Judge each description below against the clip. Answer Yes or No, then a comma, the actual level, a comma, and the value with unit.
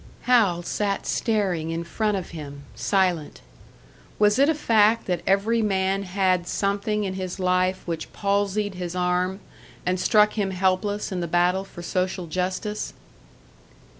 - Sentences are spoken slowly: No, average, 145 wpm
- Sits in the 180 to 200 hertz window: Yes, high, 190 Hz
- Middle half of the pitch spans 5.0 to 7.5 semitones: No, narrow, 2.4 semitones